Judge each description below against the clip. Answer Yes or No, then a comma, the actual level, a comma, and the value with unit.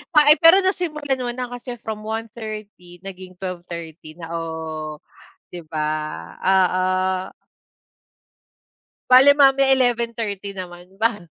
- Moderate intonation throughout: No, wide, 5.9 semitones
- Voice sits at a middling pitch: No, high, 215 Hz